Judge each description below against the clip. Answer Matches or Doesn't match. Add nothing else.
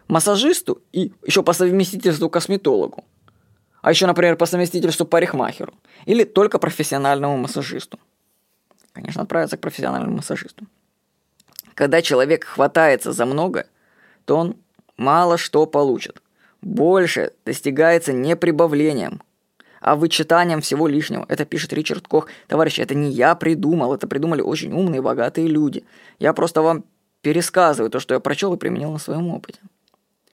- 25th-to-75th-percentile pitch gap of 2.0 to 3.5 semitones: Matches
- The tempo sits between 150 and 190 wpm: Doesn't match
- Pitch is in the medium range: Matches